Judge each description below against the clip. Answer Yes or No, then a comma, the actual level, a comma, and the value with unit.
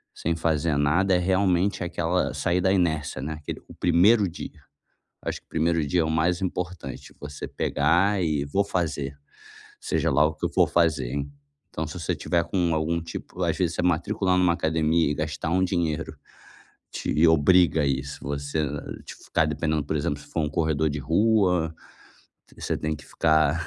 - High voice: No, very low, 80 Hz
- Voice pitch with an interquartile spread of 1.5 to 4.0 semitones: Yes, average, 2.8 semitones